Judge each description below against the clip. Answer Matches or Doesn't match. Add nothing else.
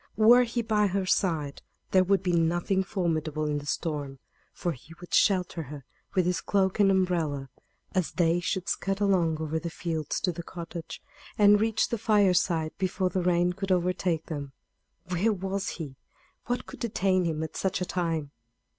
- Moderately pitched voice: Matches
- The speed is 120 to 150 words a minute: Doesn't match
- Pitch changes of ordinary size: Matches